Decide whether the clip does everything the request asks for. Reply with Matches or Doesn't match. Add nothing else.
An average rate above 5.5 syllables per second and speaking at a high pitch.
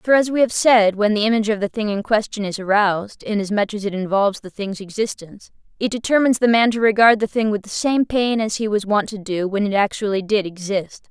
Matches